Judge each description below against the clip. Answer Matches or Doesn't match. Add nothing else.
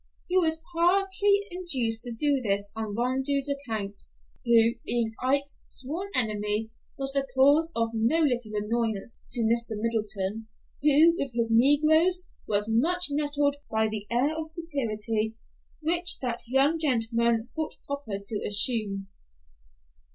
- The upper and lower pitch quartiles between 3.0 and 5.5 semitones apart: Matches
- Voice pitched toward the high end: Matches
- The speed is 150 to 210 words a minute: Doesn't match